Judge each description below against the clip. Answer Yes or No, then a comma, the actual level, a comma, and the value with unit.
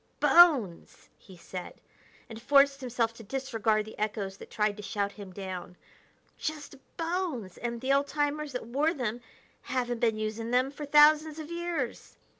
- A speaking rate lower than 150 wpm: No, average, 160 wpm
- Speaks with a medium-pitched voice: No, high, 245 Hz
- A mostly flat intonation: No, wide, 5.4 semitones